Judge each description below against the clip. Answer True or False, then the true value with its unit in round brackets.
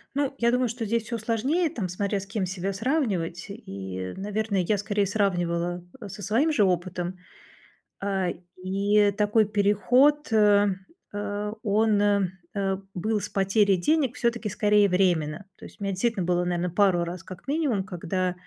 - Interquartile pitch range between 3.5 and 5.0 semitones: False (3.0 semitones)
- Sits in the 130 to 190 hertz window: False (200 Hz)